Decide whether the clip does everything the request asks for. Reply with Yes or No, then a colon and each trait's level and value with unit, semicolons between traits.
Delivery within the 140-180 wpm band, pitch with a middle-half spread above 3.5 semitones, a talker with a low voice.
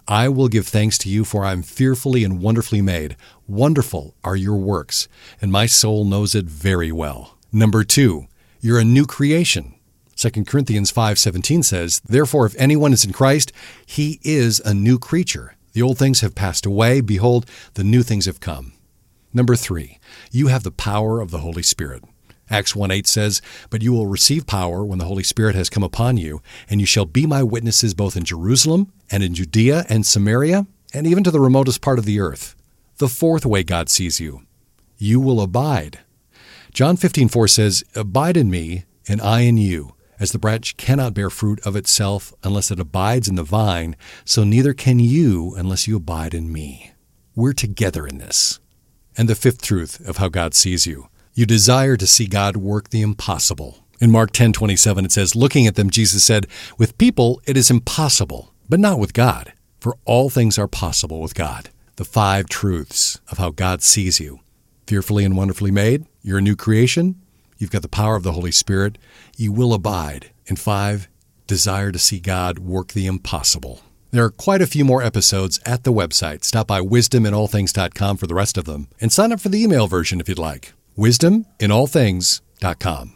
No: average, 190 wpm; average, 4.3 semitones; low, 105 Hz